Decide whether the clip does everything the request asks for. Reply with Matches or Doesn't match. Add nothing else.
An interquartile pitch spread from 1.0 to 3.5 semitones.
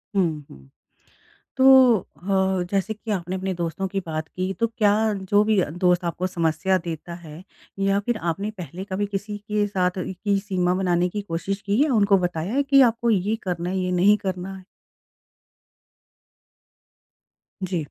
Matches